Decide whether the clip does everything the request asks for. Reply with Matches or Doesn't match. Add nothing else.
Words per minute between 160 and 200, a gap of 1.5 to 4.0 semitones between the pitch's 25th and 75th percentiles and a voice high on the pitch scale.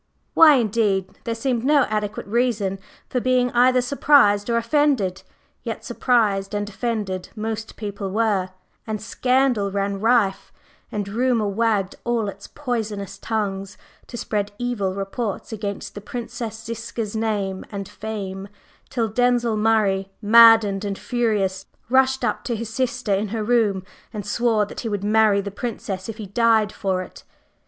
Doesn't match